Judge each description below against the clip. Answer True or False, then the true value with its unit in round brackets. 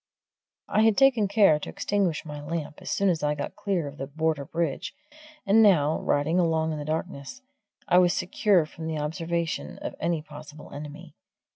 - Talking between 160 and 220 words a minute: True (180 wpm)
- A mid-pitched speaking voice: True (160 Hz)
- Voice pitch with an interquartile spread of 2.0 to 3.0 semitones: False (3.5 semitones)